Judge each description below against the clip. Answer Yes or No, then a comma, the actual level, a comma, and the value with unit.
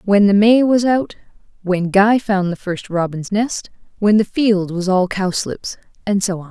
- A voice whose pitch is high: Yes, high, 200 Hz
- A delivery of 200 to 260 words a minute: No, average, 165 wpm